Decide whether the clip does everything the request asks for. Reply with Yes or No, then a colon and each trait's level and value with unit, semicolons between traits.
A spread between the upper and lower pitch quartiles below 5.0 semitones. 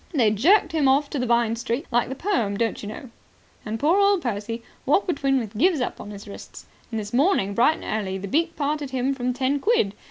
No: average, 5.3 semitones